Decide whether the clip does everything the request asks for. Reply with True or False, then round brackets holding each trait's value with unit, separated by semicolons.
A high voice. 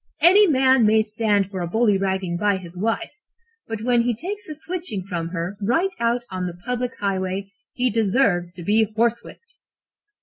True (215 Hz)